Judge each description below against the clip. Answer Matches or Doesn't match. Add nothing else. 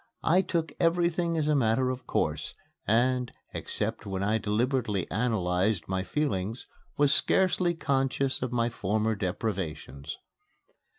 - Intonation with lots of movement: Matches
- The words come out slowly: Matches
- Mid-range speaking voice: Doesn't match